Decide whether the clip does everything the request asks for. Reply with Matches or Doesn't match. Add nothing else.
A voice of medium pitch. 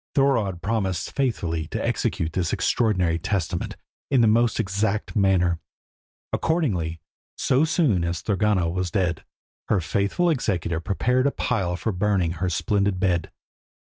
Doesn't match